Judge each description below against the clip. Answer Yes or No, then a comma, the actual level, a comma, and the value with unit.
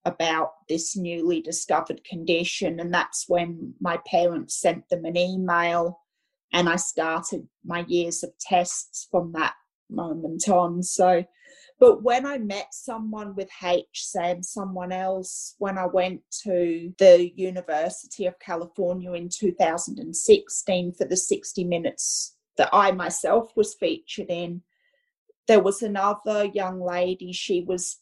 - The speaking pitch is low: No, medium, 180 Hz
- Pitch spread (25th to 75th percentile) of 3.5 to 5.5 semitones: No, narrow, 2.6 semitones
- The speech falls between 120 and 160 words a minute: Yes, slow, 135 wpm